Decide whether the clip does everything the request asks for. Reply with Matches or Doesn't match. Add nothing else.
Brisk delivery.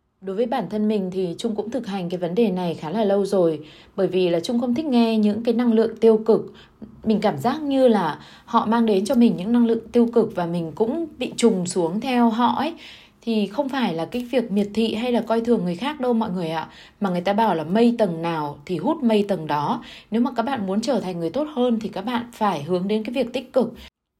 Matches